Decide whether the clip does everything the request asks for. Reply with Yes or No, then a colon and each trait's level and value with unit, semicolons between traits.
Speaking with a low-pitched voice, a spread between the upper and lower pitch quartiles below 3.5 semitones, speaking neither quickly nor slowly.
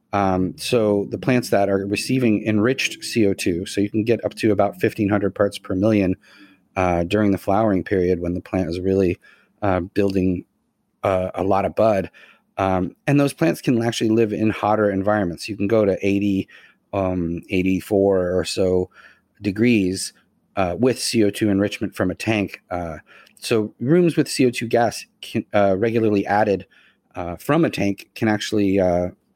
Yes: low, 100 Hz; average, 2.7 semitones; average, 165 wpm